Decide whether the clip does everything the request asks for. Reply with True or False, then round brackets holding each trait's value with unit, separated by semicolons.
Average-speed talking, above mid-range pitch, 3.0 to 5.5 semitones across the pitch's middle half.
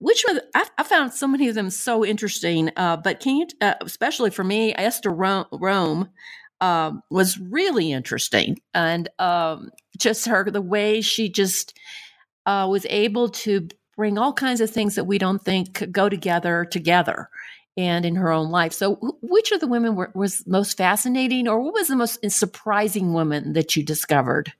True (190 wpm; 200 Hz; 4.2 semitones)